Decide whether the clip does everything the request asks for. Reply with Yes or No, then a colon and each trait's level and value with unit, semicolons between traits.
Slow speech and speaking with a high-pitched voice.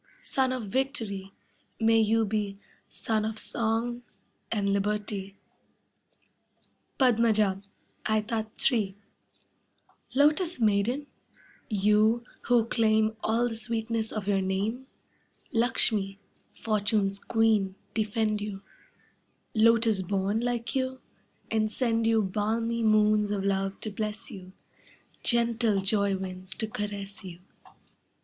Yes: slow, 105 wpm; high, 215 Hz